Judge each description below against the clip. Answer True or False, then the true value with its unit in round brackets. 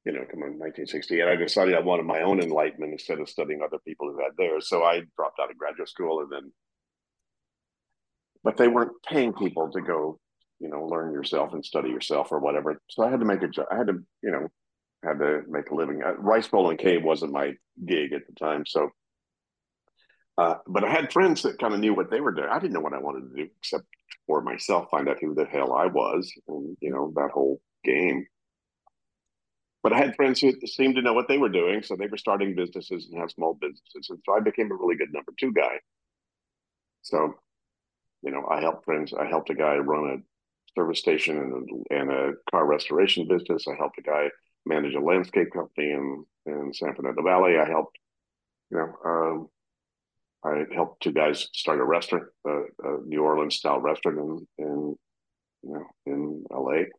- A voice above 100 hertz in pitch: False (75 Hz)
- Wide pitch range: True (8.1 semitones)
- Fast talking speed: True (210 wpm)